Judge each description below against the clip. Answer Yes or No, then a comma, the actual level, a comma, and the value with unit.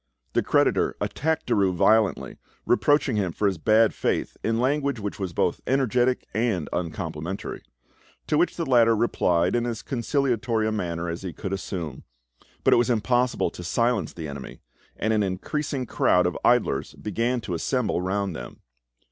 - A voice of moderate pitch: No, low, 110 Hz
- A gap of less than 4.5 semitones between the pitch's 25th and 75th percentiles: No, wide, 5.4 semitones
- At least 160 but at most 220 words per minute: Yes, average, 165 wpm